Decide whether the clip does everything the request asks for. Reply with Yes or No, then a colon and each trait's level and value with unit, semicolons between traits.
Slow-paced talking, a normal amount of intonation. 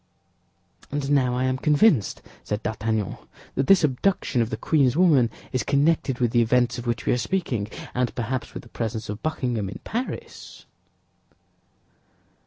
No: average, 160 wpm; average, 3.9 semitones